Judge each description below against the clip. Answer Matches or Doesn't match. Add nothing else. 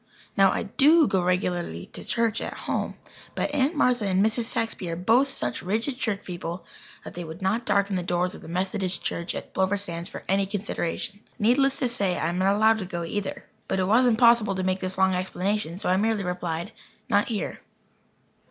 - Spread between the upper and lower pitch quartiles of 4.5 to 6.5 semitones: Doesn't match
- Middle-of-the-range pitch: Doesn't match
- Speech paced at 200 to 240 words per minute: Matches